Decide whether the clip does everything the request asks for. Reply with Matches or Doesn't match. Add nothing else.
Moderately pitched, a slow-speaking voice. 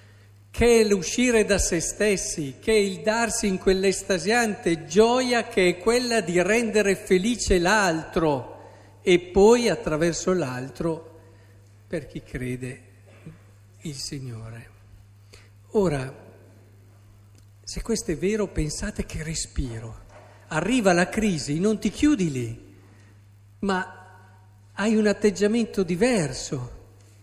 Matches